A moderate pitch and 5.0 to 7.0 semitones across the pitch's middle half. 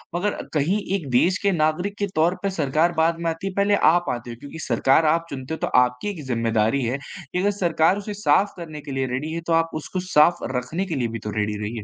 Yes: medium, 160 Hz; average, 5.3 semitones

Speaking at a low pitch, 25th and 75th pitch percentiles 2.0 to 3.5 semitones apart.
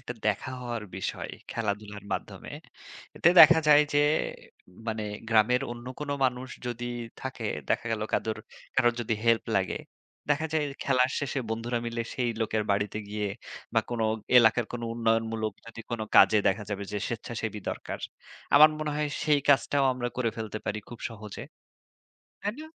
Yes: low, 115 Hz; average, 2.8 semitones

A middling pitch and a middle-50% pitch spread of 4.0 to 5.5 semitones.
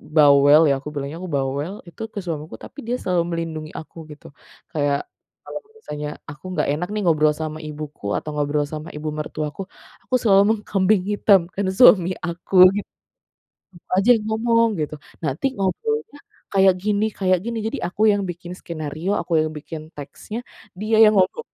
Yes: medium, 170 Hz; average, 5.2 semitones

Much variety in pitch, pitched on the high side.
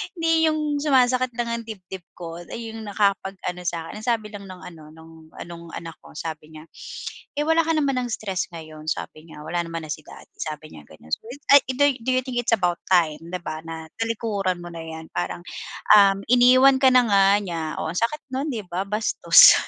Yes: wide, 6.9 semitones; high, 195 Hz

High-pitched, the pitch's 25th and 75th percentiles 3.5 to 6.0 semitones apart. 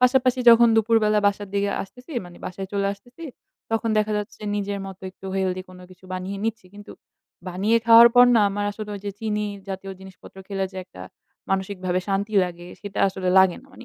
No: high, 200 Hz; average, 2.8 semitones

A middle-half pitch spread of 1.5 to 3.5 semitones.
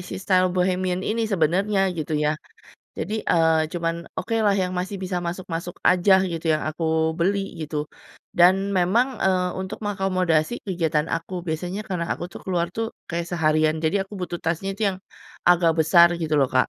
Yes: average, 2.8 semitones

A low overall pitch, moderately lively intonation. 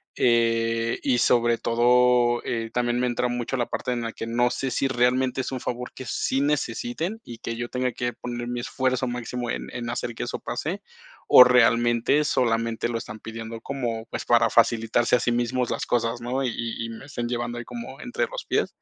No: low, 120 Hz; narrow, 1.3 semitones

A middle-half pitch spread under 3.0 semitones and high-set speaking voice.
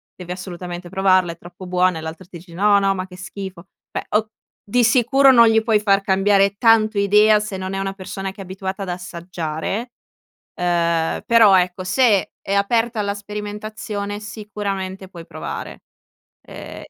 Yes: narrow, 2.5 semitones; high, 195 Hz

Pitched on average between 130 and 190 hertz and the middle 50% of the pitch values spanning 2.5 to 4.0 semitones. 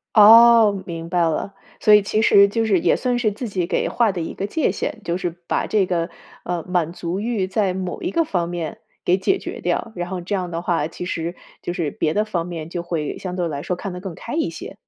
Yes: medium, 185 Hz; average, 3.7 semitones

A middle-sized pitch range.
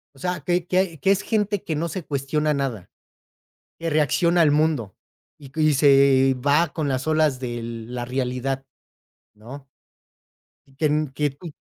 Yes: average, 3.5 semitones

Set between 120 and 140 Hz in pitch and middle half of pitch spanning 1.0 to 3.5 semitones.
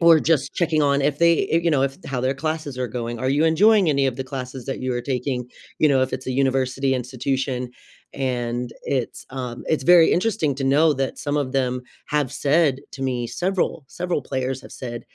Yes: low, 135 Hz; average, 2.9 semitones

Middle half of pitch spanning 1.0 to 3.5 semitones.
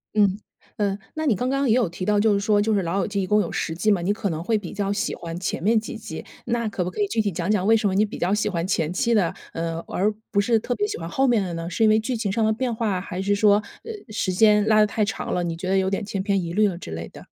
Yes: average, 2.9 semitones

